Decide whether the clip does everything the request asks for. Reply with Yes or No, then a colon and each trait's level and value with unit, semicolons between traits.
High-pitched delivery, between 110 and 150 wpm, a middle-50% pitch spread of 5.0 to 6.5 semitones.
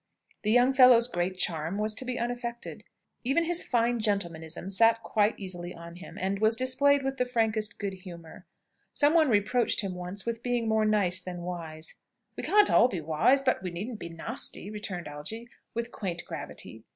No: high, 215 Hz; average, 185 wpm; average, 5.3 semitones